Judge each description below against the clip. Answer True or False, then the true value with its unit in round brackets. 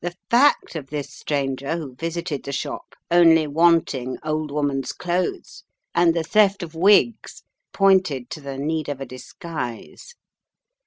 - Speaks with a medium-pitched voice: True (160 Hz)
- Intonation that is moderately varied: True (3.8 semitones)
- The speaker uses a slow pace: False (145 wpm)